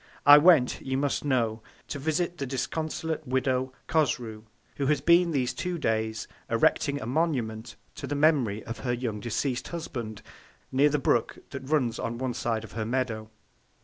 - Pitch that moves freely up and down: No, average, 4.4 semitones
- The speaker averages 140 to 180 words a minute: Yes, average, 170 wpm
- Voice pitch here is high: No, low, 130 Hz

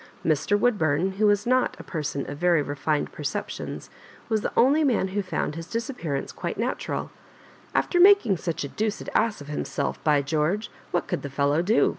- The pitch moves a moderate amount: No, wide, 6.7 semitones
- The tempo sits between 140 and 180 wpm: No, average, 200 wpm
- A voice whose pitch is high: No, medium, 180 Hz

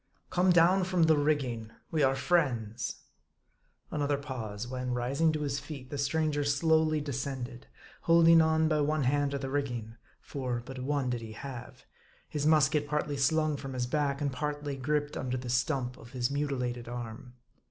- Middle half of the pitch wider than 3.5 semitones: No, average, 3.2 semitones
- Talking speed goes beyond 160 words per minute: Yes, average, 175 wpm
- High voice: No, medium, 140 Hz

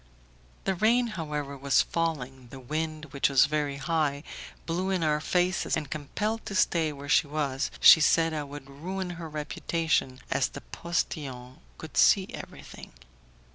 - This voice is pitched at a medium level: Yes, medium, 155 Hz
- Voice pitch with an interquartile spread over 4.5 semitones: No, average, 3.2 semitones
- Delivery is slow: No, average, 155 wpm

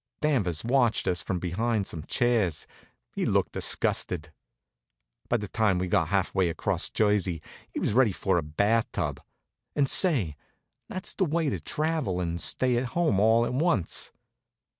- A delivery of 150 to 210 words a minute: Yes, average, 160 wpm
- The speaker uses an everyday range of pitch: No, wide, 6.1 semitones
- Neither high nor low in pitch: No, low, 105 Hz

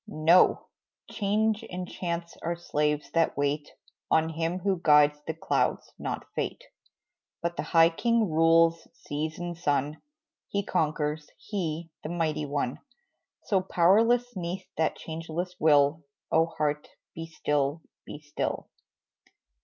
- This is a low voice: No, medium, 165 Hz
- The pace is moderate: No, slow, 130 wpm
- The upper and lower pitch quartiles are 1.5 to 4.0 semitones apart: Yes, average, 2.9 semitones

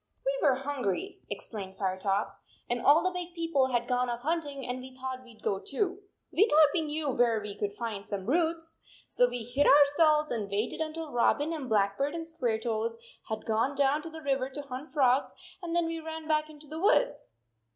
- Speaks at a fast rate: Yes, fast, 210 wpm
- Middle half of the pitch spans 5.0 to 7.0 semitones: Yes, average, 5.3 semitones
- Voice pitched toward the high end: Yes, very high, 275 Hz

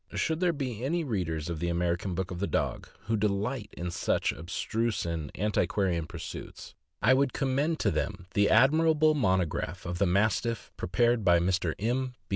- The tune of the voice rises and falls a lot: Yes, wide, 6.7 semitones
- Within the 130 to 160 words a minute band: No, average, 175 wpm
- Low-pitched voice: Yes, low, 100 Hz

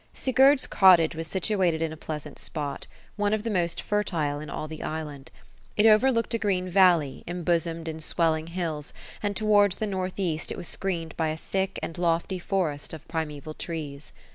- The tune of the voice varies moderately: Yes, average, 3.7 semitones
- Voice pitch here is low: No, medium, 170 Hz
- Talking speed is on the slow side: No, average, 180 wpm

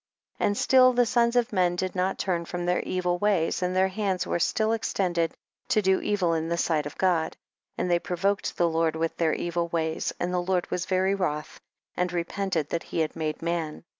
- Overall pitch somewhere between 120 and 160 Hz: No, medium, 180 Hz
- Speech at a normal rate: No, fast, 215 wpm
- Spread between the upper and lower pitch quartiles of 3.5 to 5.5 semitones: No, narrow, 2.4 semitones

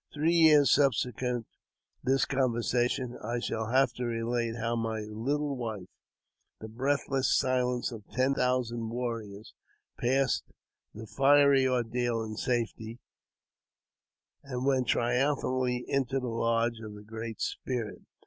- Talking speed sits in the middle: No, slow, 120 wpm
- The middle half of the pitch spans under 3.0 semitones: Yes, narrow, 2.5 semitones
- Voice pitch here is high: No, low, 120 Hz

